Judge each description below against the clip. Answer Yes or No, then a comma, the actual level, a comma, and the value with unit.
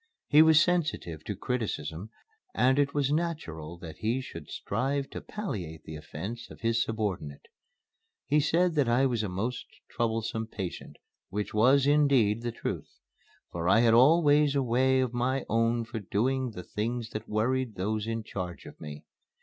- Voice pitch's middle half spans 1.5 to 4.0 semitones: No, average, 4.5 semitones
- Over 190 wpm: No, average, 165 wpm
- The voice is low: Yes, low, 115 Hz